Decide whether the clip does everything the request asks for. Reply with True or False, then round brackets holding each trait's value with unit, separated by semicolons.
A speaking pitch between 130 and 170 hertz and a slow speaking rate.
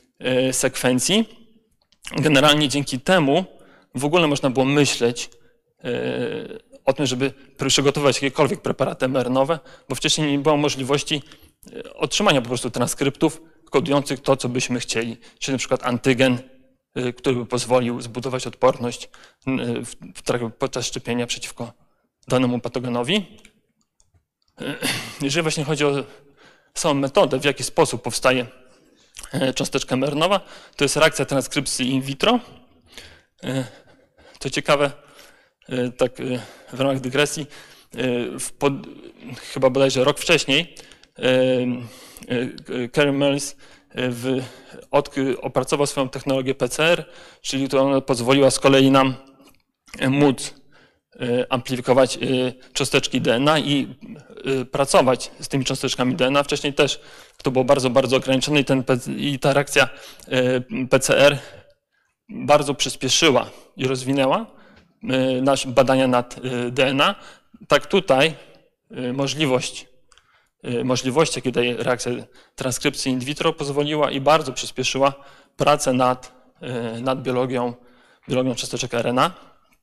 True (135 Hz; 105 wpm)